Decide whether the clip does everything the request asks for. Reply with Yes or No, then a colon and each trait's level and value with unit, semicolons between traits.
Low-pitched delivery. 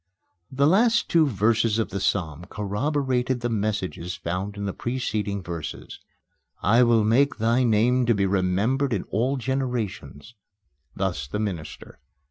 Yes: low, 110 Hz